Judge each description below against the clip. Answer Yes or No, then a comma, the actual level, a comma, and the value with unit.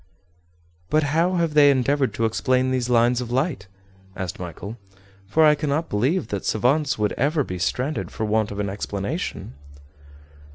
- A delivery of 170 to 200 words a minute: No, average, 160 wpm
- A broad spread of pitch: Yes, wide, 6.1 semitones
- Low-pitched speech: Yes, low, 125 Hz